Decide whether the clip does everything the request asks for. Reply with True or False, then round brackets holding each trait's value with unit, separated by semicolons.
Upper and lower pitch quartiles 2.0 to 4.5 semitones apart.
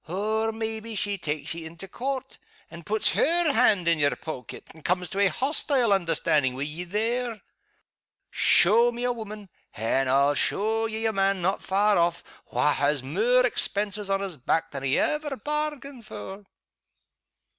False (5.4 semitones)